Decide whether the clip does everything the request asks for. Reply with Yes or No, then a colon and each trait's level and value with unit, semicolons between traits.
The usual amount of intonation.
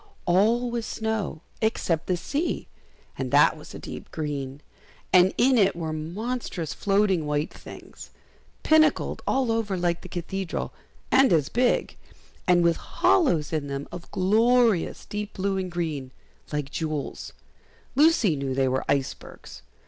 No: wide, 6.2 semitones